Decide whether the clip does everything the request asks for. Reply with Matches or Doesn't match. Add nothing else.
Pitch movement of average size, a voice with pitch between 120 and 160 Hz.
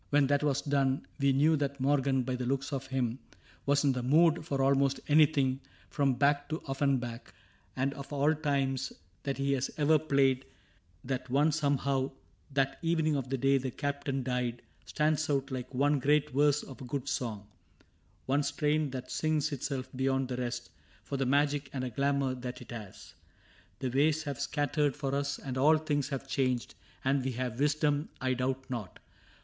Doesn't match